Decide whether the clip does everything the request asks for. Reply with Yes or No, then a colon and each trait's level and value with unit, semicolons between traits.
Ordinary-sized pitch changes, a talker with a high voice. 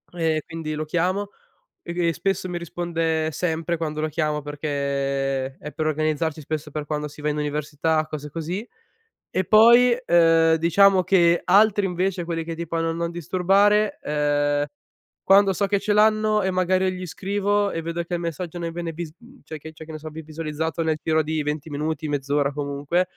No: average, 3.2 semitones; medium, 165 Hz